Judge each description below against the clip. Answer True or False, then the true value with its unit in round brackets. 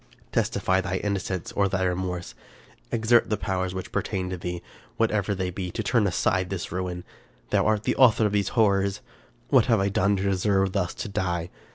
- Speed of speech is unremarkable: True (195 wpm)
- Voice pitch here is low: True (95 Hz)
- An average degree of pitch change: False (2.1 semitones)